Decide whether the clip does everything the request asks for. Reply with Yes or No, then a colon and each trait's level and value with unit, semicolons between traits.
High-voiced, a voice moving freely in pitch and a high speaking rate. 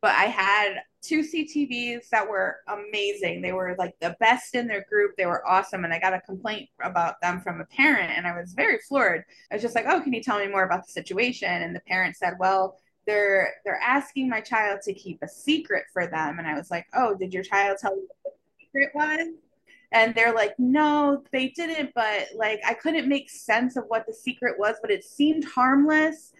Yes: high, 215 Hz; wide, 6.7 semitones; fast, 225 wpm